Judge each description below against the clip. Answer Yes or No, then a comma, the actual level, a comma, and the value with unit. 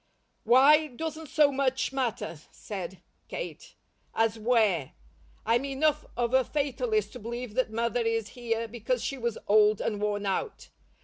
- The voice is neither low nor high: No, high, 240 Hz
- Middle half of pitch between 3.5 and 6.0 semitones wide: Yes, average, 4.0 semitones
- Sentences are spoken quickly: No, average, 145 wpm